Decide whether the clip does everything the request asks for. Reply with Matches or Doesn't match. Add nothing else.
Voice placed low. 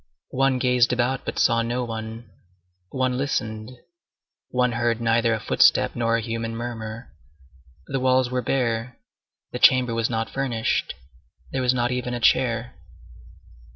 Matches